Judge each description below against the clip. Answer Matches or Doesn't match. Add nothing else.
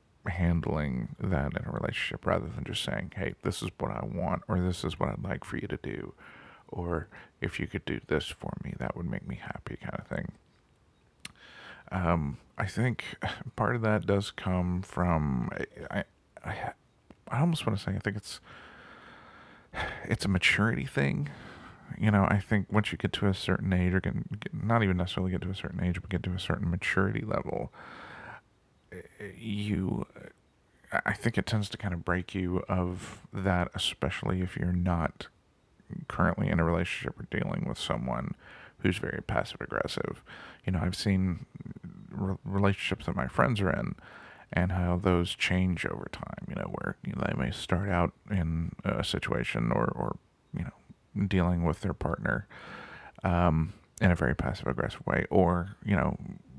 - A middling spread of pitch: Doesn't match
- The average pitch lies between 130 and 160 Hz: Doesn't match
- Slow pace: Doesn't match